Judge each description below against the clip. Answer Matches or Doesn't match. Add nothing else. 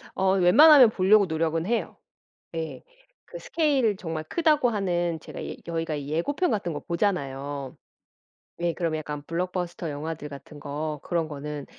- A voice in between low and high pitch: Matches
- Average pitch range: Matches